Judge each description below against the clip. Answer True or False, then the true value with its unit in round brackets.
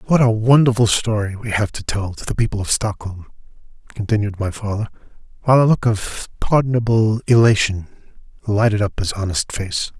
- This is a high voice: False (110 Hz)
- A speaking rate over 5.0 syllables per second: True (5.3 syllables/s)